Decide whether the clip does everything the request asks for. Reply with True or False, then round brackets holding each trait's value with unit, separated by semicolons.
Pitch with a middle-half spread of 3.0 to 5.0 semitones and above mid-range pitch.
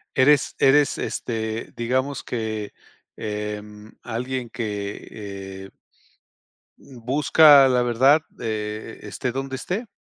False (4.1 semitones; 120 Hz)